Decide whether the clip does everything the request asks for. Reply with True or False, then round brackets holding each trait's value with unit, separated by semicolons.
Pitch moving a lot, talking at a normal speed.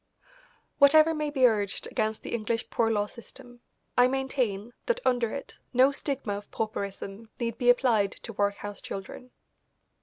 False (4.3 semitones; 150 wpm)